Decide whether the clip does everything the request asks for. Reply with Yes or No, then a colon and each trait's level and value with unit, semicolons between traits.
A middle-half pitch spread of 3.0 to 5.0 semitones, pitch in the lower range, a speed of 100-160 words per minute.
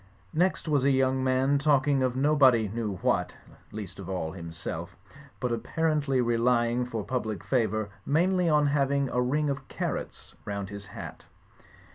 Yes: average, 4.6 semitones; low, 130 Hz; average, 155 wpm